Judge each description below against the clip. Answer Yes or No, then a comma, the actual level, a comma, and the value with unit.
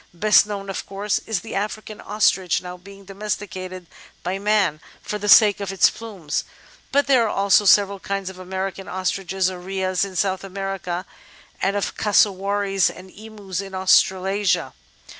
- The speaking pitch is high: Yes, high, 195 Hz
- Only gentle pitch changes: Yes, narrow, 1.6 semitones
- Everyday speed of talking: Yes, average, 160 wpm